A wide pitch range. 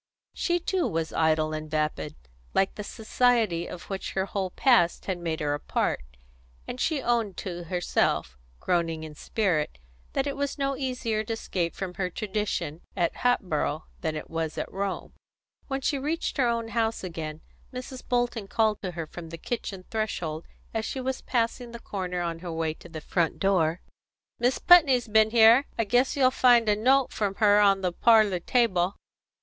Yes: wide, 6.1 semitones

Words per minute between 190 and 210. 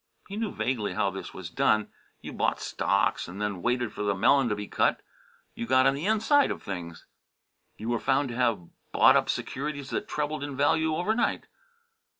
Yes: average, 195 wpm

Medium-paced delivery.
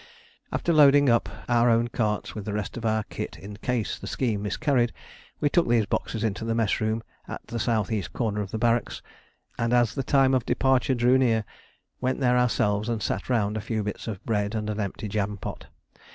No: fast, 210 wpm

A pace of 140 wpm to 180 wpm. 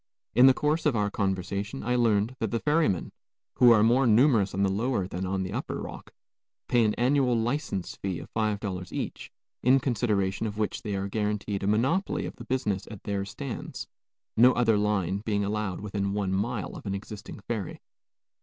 No: average, 190 wpm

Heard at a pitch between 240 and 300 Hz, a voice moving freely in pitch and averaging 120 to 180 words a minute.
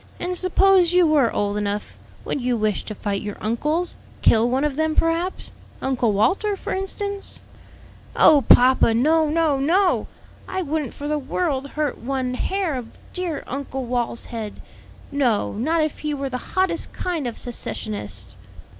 Yes: very high, 280 Hz; wide, 5.9 semitones; average, 160 wpm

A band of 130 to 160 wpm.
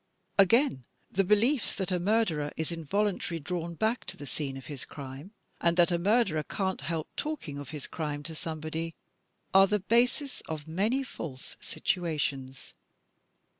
Yes: average, 155 wpm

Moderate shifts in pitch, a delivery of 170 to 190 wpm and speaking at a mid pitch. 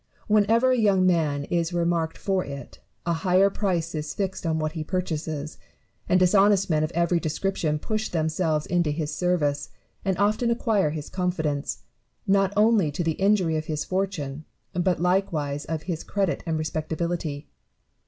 No: average, 3.8 semitones; average, 160 wpm; medium, 170 Hz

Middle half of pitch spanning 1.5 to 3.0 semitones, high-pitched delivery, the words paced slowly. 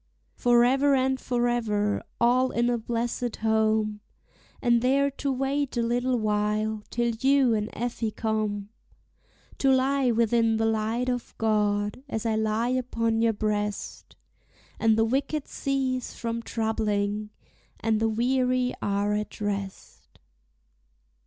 Yes: average, 2.7 semitones; high, 230 Hz; slow, 125 wpm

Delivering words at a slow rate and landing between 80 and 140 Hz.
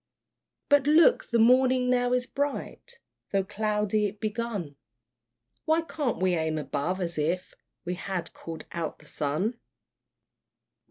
No: slow, 130 wpm; high, 210 Hz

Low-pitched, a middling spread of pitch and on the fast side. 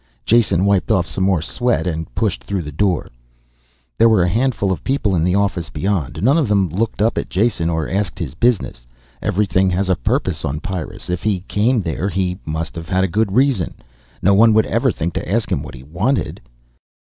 Yes: very low, 95 Hz; average, 4.3 semitones; fast, 210 wpm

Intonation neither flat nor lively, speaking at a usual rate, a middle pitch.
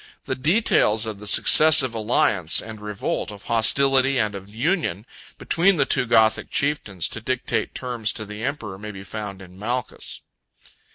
No: average, 4.3 semitones; average, 160 wpm; low, 110 Hz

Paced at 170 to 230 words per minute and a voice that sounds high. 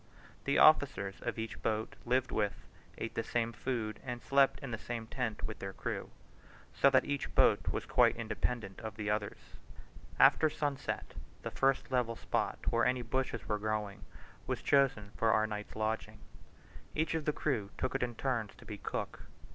No: average, 180 wpm; low, 115 Hz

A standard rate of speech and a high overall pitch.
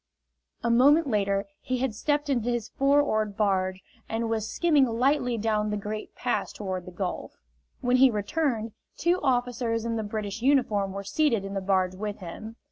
Yes: average, 180 wpm; high, 225 Hz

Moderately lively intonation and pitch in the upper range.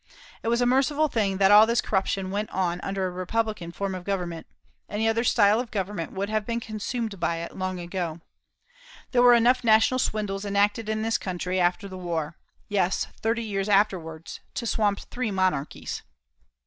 Yes: average, 3.3 semitones; high, 200 Hz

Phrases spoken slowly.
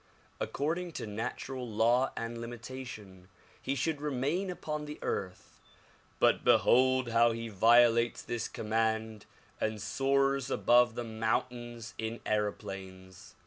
Yes: slow, 120 wpm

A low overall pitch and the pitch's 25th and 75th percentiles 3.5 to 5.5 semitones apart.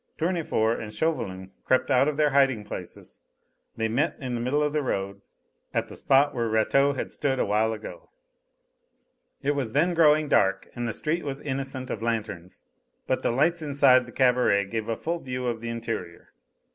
Yes: low, 125 Hz; average, 4.4 semitones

